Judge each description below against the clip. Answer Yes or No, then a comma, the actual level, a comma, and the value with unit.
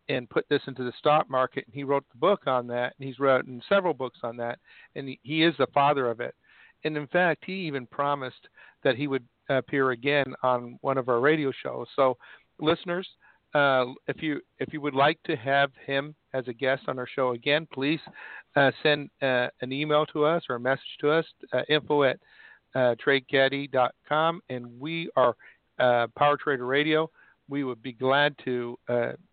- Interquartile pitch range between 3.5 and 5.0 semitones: No, average, 2.8 semitones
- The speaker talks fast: No, average, 195 wpm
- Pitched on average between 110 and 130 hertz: No, medium, 140 Hz